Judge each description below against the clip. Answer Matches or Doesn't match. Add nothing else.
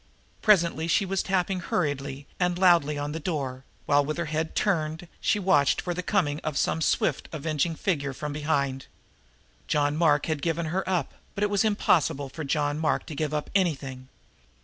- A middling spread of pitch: Matches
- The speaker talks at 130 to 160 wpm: Doesn't match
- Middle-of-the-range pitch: Matches